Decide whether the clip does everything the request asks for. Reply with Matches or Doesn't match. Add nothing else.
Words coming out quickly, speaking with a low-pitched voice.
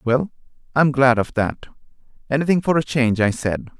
Doesn't match